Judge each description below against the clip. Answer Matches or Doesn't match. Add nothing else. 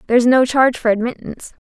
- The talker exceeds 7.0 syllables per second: Matches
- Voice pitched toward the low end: Doesn't match